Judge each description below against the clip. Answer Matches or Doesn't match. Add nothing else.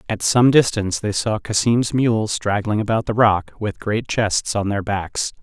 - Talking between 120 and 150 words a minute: Doesn't match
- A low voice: Matches